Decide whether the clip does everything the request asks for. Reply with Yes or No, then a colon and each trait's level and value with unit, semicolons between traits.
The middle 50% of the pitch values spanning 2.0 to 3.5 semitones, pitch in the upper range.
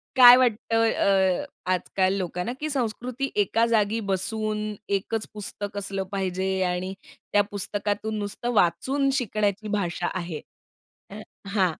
Yes: average, 3.0 semitones; high, 205 Hz